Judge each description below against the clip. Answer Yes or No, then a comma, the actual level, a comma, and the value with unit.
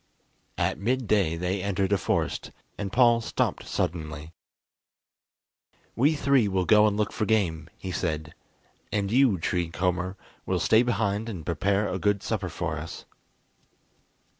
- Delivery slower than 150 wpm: Yes, average, 140 wpm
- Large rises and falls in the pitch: No, average, 3.8 semitones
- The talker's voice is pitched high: No, low, 100 Hz